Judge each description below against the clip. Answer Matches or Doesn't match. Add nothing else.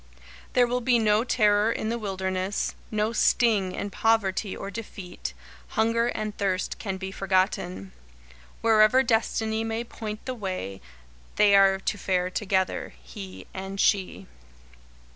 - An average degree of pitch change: Matches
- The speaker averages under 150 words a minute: Matches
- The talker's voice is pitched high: Matches